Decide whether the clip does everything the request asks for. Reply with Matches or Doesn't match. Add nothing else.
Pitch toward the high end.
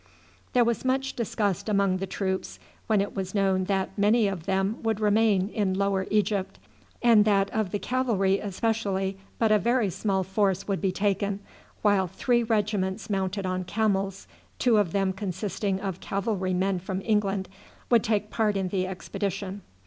Matches